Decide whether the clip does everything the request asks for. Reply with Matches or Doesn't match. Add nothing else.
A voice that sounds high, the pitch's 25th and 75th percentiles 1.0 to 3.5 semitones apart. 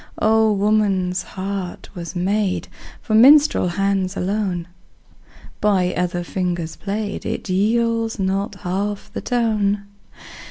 Matches